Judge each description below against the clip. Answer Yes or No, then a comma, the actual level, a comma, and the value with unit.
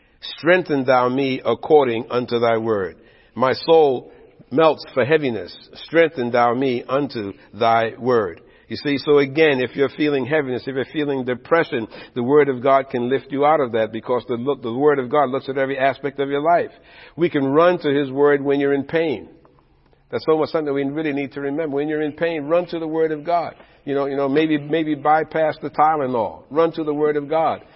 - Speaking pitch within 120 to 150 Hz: Yes, medium, 140 Hz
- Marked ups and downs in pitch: No, average, 2.8 semitones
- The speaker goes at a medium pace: No, fast, 210 wpm